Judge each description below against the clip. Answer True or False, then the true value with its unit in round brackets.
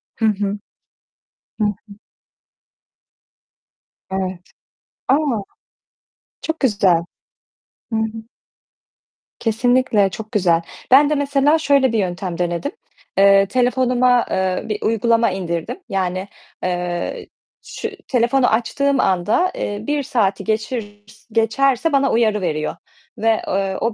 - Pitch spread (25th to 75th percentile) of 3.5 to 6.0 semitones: True (4.9 semitones)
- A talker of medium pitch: False (215 Hz)